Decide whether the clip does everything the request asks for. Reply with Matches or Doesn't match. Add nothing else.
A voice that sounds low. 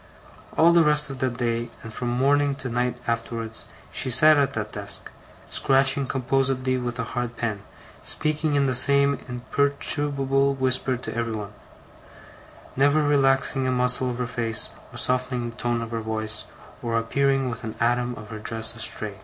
Matches